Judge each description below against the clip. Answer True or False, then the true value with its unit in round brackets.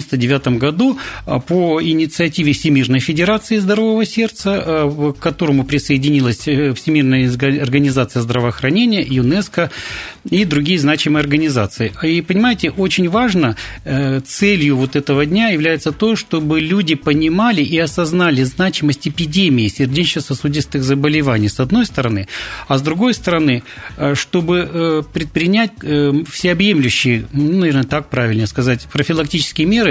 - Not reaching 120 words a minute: True (110 wpm)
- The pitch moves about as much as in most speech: True (4.4 semitones)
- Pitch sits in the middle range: True (150 Hz)